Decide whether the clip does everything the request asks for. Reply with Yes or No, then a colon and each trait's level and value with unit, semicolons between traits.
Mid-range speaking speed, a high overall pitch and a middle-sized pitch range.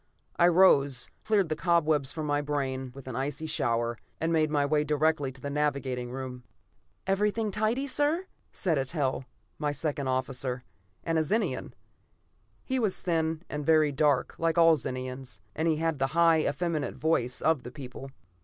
No: average, 165 wpm; medium, 150 Hz; average, 3.7 semitones